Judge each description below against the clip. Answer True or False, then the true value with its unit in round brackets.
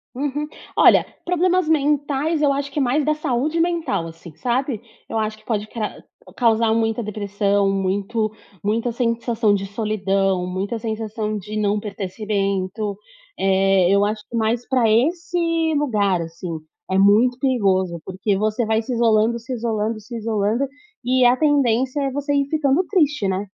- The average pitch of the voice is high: True (225 Hz)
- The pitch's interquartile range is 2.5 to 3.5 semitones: False (4.7 semitones)